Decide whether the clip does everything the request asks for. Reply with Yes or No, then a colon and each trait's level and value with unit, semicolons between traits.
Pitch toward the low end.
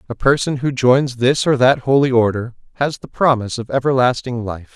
Yes: low, 125 Hz